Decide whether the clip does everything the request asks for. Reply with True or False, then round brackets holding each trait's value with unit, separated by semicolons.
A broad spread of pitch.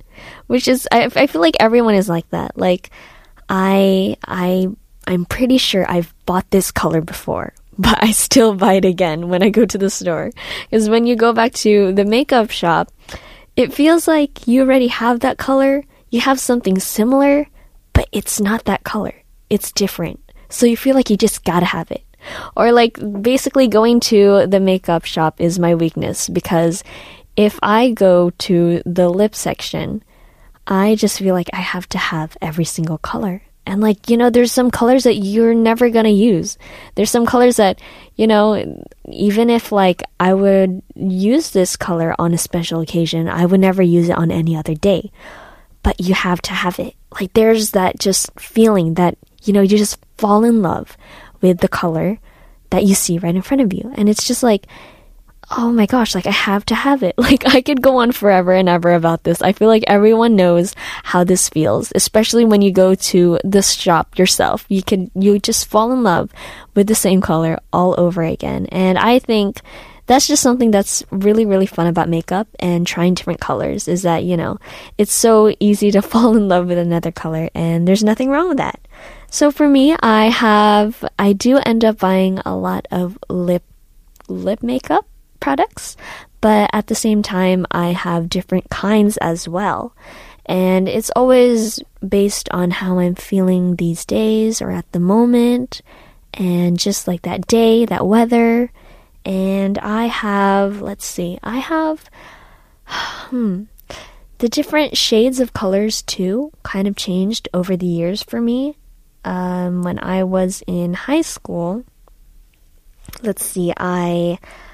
False (4.4 semitones)